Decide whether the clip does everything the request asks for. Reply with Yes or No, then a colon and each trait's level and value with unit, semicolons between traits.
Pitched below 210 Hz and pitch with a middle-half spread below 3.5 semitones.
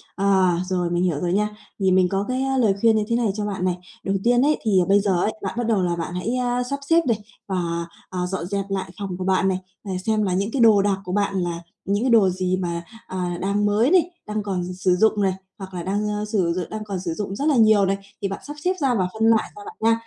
Yes: high, 200 Hz; average, 3.0 semitones